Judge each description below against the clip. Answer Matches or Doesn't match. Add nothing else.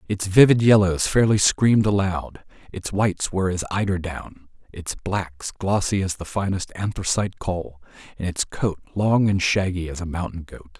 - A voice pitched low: Matches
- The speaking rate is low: Doesn't match